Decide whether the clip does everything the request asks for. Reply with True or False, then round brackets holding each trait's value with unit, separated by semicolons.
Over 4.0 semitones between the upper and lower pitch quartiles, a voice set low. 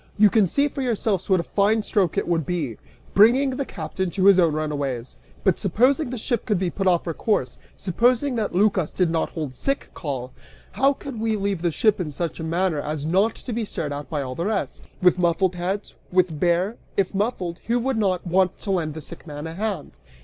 False (4.9 semitones; 185 Hz)